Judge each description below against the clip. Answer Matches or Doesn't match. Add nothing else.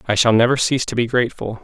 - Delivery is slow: Doesn't match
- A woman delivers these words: Doesn't match